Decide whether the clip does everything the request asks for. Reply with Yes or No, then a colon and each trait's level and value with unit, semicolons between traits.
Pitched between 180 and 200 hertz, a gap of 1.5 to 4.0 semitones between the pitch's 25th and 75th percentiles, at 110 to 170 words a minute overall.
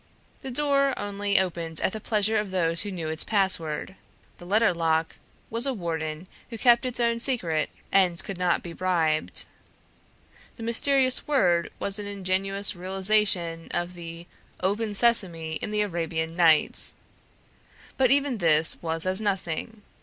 No: high, 190 Hz; average, 4.6 semitones; average, 150 wpm